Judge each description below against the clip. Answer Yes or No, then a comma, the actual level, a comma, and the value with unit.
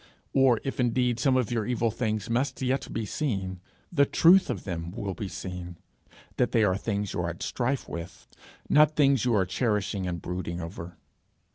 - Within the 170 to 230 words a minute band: Yes, average, 185 wpm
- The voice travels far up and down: Yes, wide, 5.7 semitones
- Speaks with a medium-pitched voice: No, low, 110 Hz